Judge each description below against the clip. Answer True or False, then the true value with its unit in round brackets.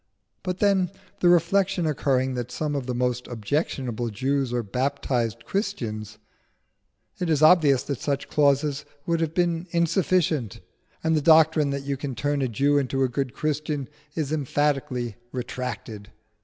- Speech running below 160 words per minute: True (150 wpm)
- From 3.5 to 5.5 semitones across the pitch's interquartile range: True (4.1 semitones)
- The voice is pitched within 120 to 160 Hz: True (140 Hz)